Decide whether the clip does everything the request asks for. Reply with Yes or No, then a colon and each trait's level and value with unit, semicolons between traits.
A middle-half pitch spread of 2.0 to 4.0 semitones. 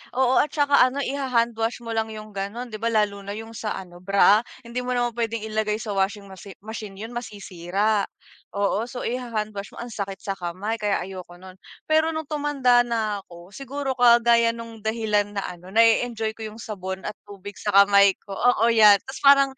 Yes: average, 3.2 semitones